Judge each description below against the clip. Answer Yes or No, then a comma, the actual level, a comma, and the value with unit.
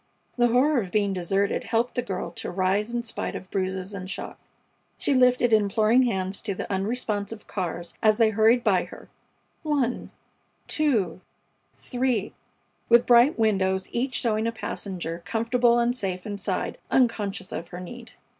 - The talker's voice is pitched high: Yes, high, 220 Hz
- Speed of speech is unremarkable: Yes, average, 155 wpm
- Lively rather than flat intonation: No, average, 4.1 semitones